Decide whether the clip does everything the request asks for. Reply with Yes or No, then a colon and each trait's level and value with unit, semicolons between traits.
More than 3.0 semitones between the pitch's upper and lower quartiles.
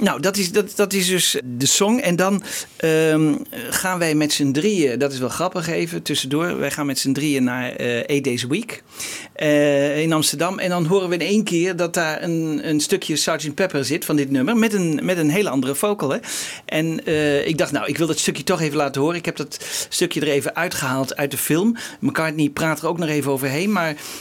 Yes: average, 4.0 semitones